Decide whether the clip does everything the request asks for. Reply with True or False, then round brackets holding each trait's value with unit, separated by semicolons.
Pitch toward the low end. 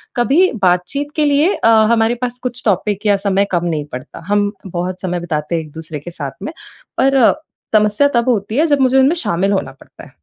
False (205 Hz)